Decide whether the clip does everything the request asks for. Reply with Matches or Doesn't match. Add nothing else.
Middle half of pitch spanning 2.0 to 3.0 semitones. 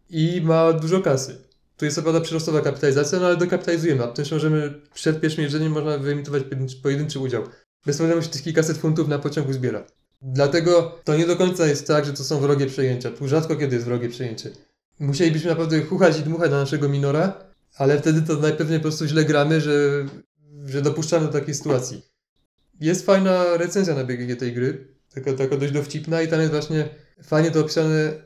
Matches